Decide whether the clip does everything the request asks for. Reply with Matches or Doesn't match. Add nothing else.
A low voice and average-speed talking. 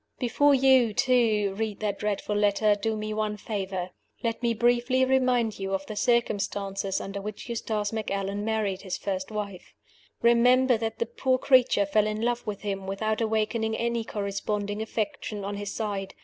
Doesn't match